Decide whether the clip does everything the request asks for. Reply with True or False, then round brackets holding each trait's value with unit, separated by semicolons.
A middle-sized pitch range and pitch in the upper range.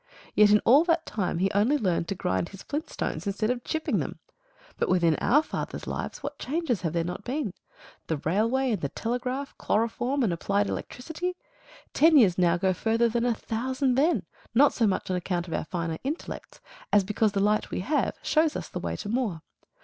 False (6.4 semitones; 220 Hz)